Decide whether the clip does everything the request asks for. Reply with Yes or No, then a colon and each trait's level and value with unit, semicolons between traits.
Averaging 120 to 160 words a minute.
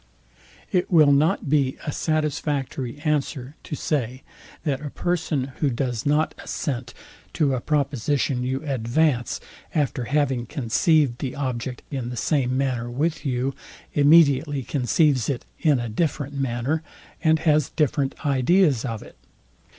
Yes: slow, 135 wpm